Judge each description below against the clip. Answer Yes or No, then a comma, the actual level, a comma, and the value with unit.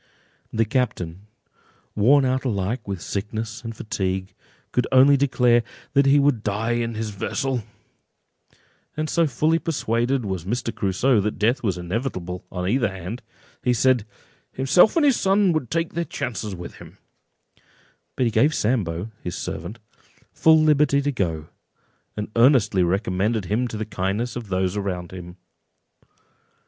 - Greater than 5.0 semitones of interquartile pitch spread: Yes, wide, 5.4 semitones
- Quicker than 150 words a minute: No, average, 145 wpm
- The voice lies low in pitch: Yes, low, 115 Hz